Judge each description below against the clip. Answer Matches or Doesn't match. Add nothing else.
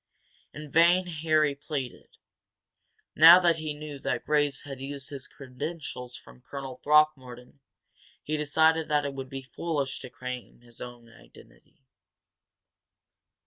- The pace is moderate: Doesn't match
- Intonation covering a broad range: Doesn't match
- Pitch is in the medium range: Matches